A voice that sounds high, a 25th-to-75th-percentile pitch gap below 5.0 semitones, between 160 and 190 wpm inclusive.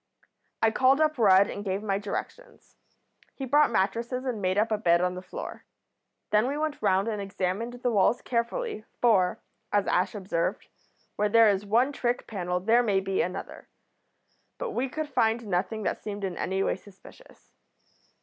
Yes: high, 215 Hz; average, 4.1 semitones; average, 175 wpm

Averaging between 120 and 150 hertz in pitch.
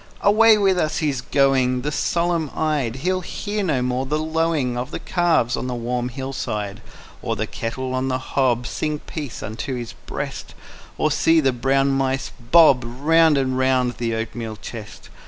Yes: low, 135 Hz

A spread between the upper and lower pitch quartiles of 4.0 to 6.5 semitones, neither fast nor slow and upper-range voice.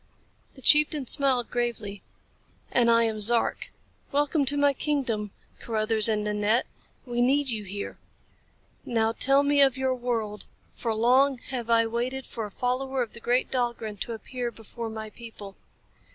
No: average, 3.2 semitones; average, 155 wpm; high, 240 Hz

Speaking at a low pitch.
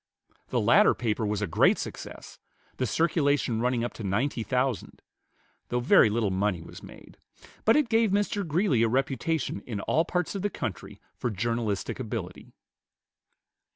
Yes: low, 125 Hz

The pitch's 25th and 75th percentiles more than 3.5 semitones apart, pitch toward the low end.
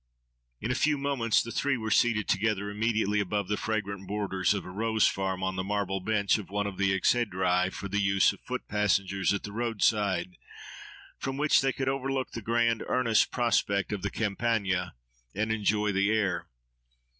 No: average, 2.9 semitones; low, 105 Hz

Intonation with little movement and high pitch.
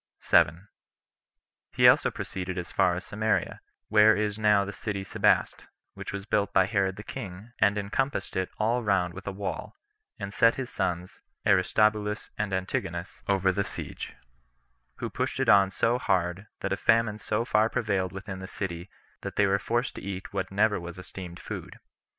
No: narrow, 2.2 semitones; low, 100 Hz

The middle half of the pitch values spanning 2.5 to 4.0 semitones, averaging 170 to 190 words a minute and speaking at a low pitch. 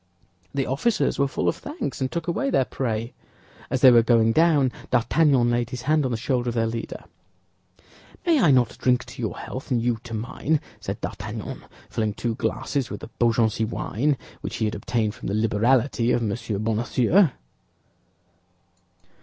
Yes: average, 3.3 semitones; average, 175 wpm; low, 120 Hz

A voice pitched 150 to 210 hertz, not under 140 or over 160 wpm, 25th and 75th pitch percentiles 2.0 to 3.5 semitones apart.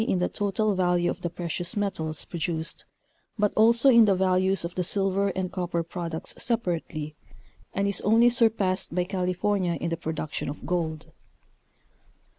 Yes: medium, 185 Hz; average, 155 wpm; average, 3.0 semitones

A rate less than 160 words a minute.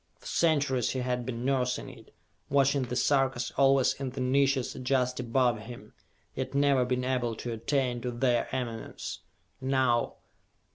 Yes: average, 150 wpm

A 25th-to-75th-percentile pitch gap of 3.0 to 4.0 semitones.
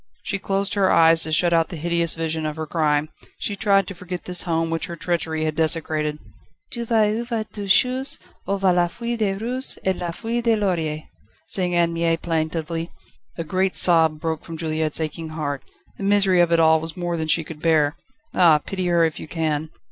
Yes: average, 3.3 semitones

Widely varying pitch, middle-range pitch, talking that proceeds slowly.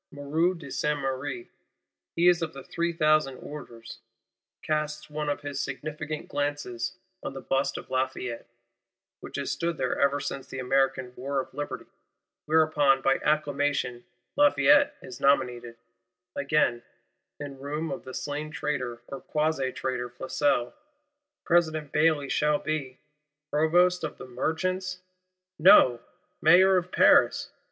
No: average, 2.7 semitones; medium, 145 Hz; slow, 130 wpm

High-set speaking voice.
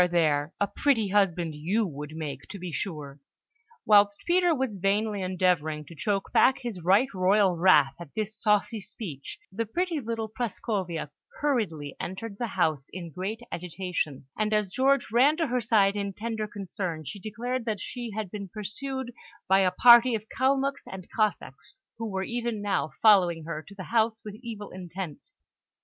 Yes: high, 205 Hz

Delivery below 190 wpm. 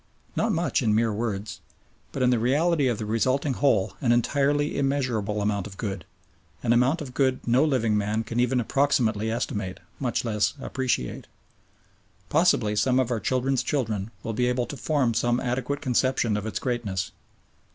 Yes: average, 170 wpm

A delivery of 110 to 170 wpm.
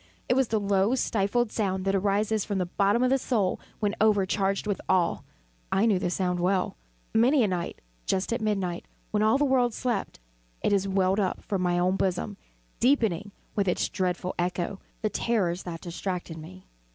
No: average, 185 wpm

